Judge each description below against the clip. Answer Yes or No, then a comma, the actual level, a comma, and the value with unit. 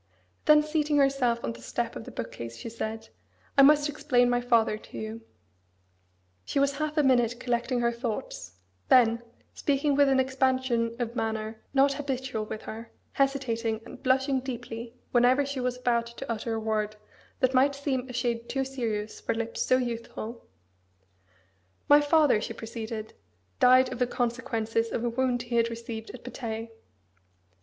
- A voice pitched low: No, high, 245 Hz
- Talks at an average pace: Yes, average, 165 wpm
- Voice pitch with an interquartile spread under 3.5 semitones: Yes, average, 2.8 semitones